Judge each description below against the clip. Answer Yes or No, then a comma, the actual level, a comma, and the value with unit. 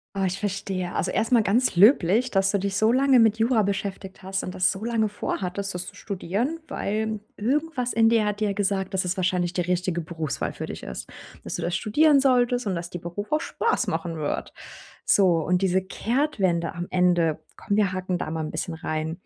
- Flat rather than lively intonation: No, average, 3.8 semitones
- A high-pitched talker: Yes, high, 195 Hz